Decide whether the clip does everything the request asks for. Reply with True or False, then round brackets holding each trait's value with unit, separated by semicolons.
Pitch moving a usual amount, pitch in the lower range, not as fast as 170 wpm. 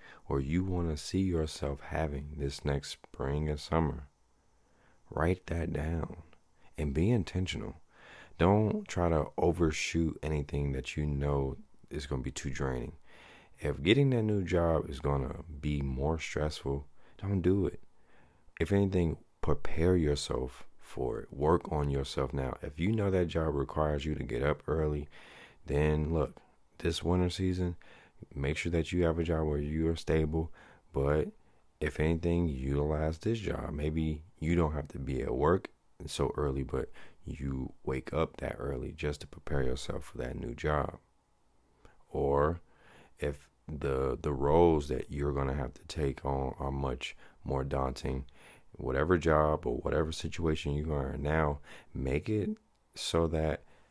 True (3.1 semitones; 75 Hz; 160 wpm)